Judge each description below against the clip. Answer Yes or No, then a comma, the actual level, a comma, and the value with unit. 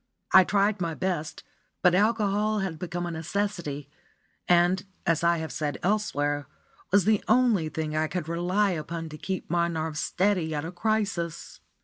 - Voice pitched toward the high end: No, medium, 175 Hz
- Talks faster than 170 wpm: No, average, 160 wpm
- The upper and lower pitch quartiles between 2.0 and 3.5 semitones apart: No, average, 3.9 semitones